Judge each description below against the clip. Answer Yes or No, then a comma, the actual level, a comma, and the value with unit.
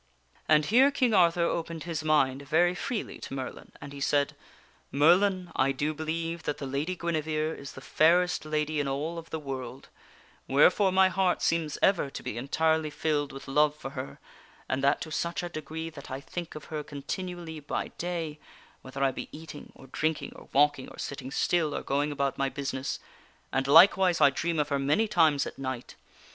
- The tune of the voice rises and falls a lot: No, average, 3.3 semitones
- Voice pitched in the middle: Yes, medium, 155 Hz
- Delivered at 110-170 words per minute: No, average, 195 wpm